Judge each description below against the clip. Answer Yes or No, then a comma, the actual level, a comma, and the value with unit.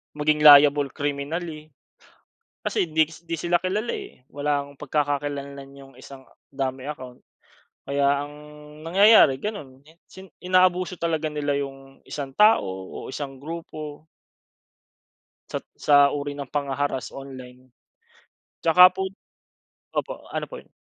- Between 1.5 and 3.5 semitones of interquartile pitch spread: Yes, average, 3.1 semitones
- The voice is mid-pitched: Yes, medium, 145 Hz